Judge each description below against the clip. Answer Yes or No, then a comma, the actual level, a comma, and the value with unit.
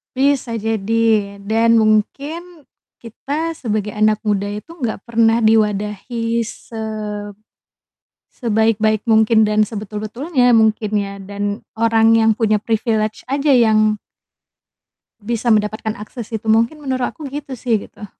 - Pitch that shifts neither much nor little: No, narrow, 1.8 semitones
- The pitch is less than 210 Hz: No, high, 225 Hz